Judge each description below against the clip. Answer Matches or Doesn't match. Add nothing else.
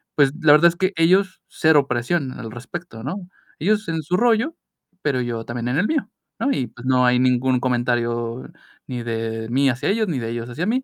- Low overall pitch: Matches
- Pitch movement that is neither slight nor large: Doesn't match